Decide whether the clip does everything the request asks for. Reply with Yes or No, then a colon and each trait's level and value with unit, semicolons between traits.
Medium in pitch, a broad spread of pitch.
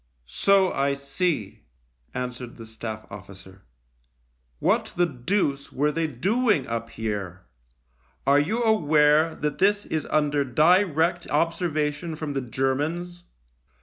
Yes: medium, 145 Hz; wide, 6.4 semitones